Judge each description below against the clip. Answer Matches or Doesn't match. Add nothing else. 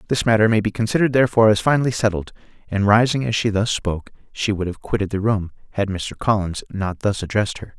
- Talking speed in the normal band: Doesn't match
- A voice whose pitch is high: Doesn't match